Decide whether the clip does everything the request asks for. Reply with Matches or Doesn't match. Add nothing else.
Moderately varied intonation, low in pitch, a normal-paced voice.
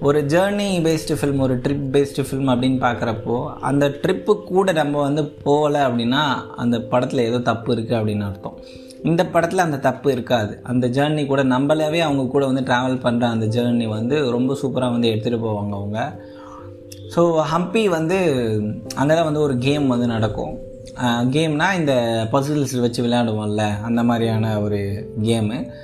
Doesn't match